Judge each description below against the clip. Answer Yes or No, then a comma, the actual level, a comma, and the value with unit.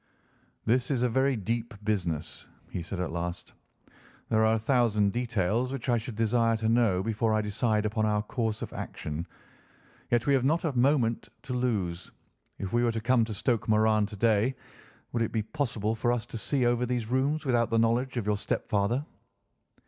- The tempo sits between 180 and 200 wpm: Yes, average, 195 wpm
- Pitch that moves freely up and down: No, narrow, 2.5 semitones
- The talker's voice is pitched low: Yes, low, 115 Hz